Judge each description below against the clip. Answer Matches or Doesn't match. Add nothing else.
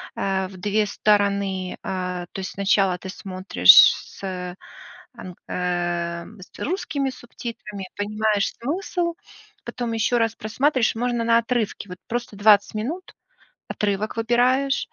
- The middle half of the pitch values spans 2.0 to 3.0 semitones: Doesn't match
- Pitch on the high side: Matches